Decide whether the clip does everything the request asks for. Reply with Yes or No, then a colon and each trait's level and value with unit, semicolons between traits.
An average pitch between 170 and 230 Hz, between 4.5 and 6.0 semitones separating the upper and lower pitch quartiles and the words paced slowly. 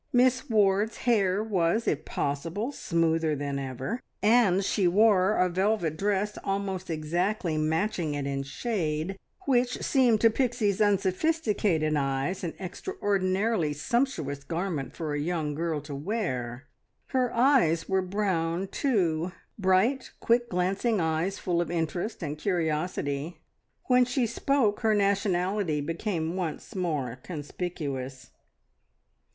Yes: medium, 185 Hz; average, 5.2 semitones; slow, 125 wpm